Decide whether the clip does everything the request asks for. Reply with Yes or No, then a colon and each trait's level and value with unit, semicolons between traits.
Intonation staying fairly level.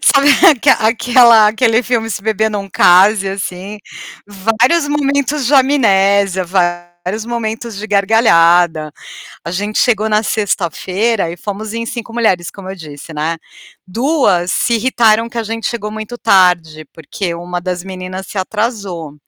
No: average, 4.1 semitones